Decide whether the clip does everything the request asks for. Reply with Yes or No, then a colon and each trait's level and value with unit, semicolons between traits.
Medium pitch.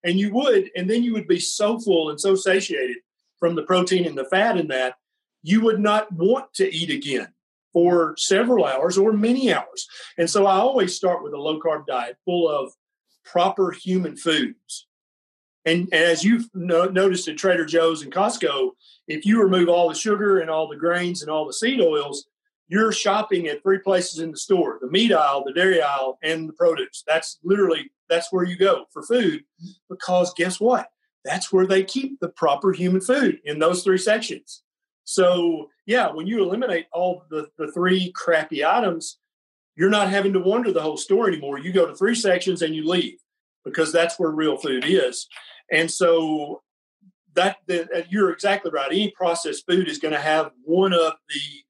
Yes: medium, 180 Hz